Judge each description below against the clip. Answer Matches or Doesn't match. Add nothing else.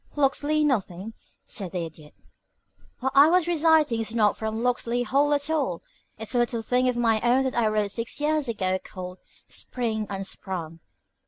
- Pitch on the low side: Doesn't match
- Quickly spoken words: Doesn't match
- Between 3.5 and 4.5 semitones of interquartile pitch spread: Doesn't match